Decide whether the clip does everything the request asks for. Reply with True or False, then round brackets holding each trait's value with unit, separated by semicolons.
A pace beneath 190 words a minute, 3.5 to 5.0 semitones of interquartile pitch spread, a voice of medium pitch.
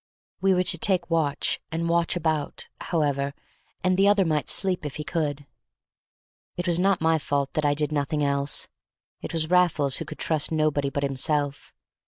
False (180 wpm; 3.1 semitones; 155 Hz)